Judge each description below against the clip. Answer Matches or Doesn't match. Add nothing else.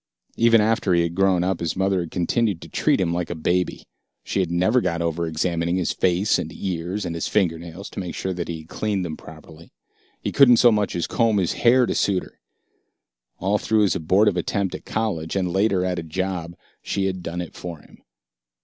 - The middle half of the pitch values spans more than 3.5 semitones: Doesn't match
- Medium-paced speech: Doesn't match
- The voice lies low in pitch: Matches